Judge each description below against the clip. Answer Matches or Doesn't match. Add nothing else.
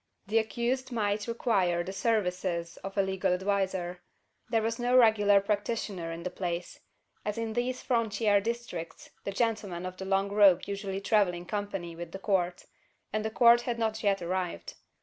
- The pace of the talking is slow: Doesn't match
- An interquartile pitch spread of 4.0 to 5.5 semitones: Doesn't match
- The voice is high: Matches